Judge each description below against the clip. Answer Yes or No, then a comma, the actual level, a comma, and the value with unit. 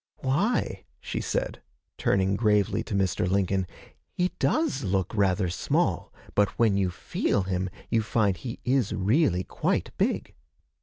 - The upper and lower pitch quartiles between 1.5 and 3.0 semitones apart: No, average, 3.4 semitones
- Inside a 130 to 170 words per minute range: Yes, average, 140 wpm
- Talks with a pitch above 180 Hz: No, low, 100 Hz